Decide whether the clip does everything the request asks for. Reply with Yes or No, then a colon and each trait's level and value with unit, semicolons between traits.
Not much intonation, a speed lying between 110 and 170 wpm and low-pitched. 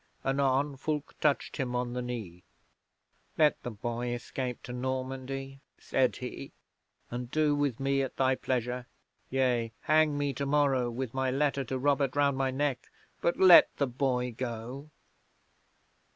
Yes: narrow, 2.2 semitones; average, 145 wpm; low, 130 Hz